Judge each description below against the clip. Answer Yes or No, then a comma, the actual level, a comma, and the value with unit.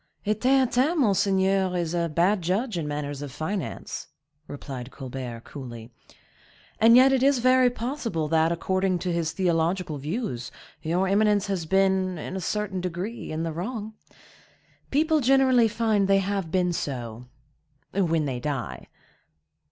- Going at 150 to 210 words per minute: No, average, 140 wpm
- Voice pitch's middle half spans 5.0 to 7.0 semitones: Yes, wide, 5.5 semitones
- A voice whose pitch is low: No, medium, 185 Hz